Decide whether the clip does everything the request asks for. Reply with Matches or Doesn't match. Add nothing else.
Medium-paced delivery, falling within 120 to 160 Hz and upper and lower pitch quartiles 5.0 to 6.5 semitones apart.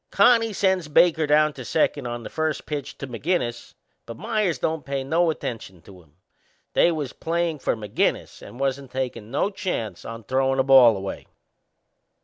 Matches